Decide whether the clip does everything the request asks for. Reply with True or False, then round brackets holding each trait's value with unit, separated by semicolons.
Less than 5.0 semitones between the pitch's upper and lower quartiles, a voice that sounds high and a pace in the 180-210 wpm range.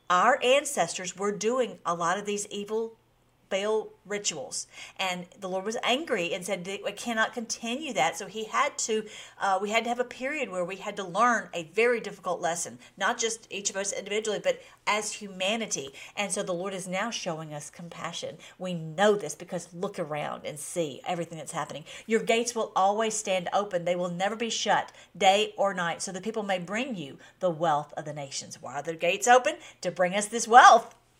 True (4.1 semitones; 200 Hz; 205 wpm)